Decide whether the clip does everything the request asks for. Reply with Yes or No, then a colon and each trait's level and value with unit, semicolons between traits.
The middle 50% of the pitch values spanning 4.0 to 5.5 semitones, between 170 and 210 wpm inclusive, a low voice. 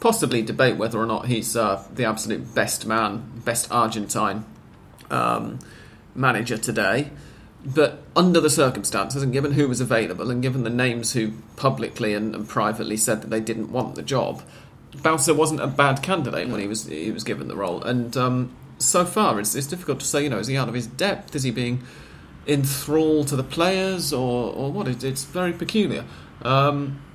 Yes: average, 4.3 semitones; average, 190 wpm; low, 125 Hz